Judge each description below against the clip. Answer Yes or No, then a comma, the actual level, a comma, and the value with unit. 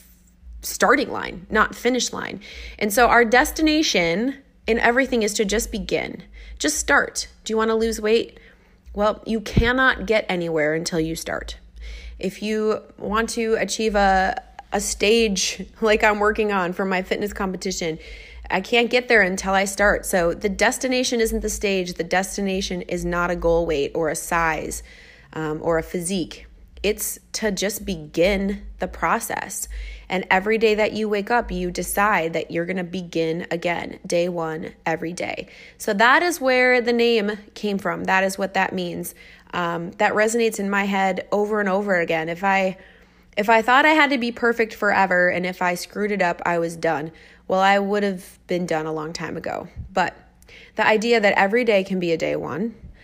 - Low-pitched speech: No, high, 200 Hz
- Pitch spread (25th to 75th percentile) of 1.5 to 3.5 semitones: No, average, 4.0 semitones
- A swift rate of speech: No, average, 185 wpm